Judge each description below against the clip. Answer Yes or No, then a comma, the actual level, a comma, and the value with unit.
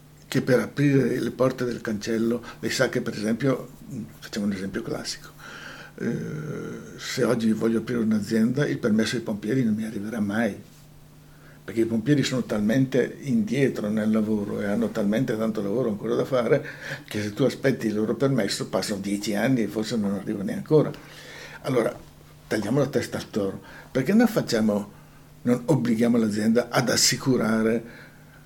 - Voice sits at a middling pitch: No, low, 115 Hz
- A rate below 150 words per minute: No, average, 160 wpm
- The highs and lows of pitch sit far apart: No, average, 3.2 semitones